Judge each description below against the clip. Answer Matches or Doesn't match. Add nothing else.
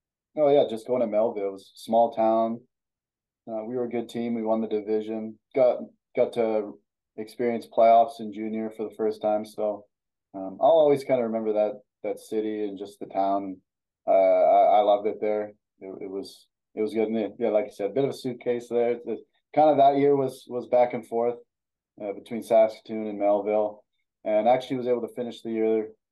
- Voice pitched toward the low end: Matches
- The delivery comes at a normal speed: Doesn't match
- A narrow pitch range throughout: Matches